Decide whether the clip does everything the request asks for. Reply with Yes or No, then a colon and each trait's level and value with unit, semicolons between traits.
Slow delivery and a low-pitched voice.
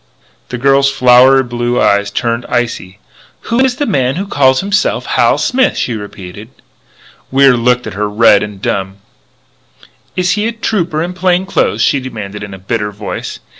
No: average, 170 wpm; low, 125 Hz